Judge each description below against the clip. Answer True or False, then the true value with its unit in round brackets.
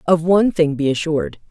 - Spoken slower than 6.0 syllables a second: False (6.3 syllables/s)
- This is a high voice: False (155 Hz)